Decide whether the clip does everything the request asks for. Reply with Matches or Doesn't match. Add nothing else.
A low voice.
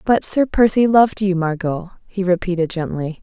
Doesn't match